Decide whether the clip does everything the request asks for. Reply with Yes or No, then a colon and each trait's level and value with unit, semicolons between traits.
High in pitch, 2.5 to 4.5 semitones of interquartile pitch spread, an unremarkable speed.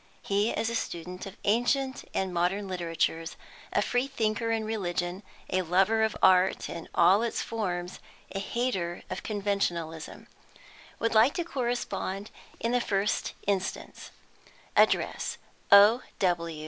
No: high, 200 Hz; average, 4.0 semitones; slow, 130 wpm